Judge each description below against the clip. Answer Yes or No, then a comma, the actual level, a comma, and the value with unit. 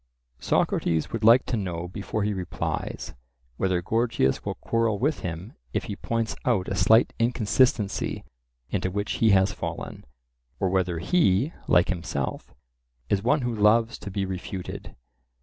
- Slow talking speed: No, average, 150 wpm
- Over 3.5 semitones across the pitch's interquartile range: Yes, average, 3.9 semitones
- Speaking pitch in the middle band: No, low, 100 Hz